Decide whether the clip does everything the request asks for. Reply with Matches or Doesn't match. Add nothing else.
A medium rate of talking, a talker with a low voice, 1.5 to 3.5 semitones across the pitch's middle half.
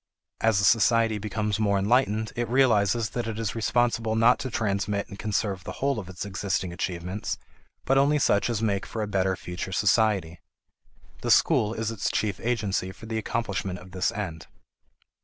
Matches